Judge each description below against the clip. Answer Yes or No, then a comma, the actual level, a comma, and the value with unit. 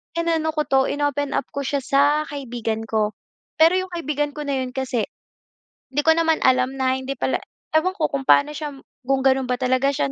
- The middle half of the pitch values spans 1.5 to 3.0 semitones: Yes, narrow, 2.6 semitones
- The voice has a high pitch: Yes, very high, 275 Hz